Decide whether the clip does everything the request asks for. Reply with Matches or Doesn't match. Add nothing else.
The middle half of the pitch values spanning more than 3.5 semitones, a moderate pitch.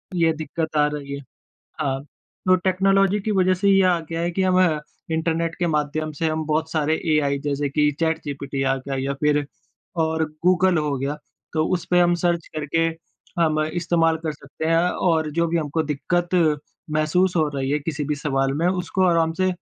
Doesn't match